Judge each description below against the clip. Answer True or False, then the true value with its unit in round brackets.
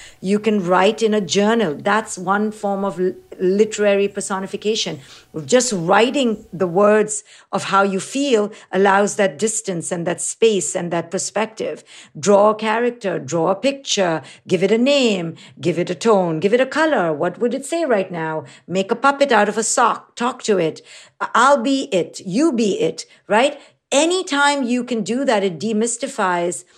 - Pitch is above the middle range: True (205 Hz)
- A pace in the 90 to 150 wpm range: False (175 wpm)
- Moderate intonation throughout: True (3.8 semitones)